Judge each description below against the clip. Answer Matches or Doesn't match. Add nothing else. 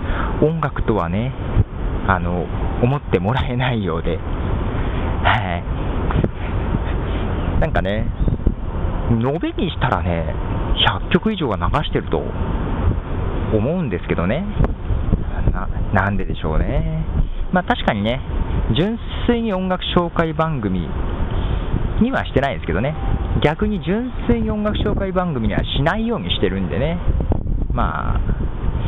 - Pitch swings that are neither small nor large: Doesn't match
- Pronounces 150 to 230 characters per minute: Matches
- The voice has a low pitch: Matches